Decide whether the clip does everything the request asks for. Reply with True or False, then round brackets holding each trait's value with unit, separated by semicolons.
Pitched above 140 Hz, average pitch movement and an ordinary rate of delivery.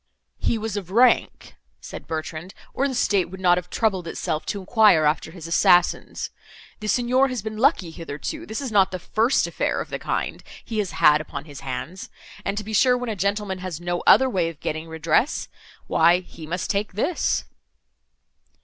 True (190 Hz; 4.8 semitones; 185 wpm)